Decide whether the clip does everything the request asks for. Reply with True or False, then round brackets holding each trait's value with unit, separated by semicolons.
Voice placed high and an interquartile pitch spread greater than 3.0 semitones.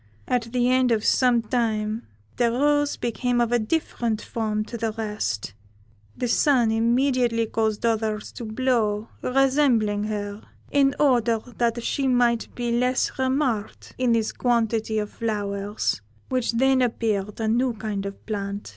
False (230 Hz; 2.6 semitones)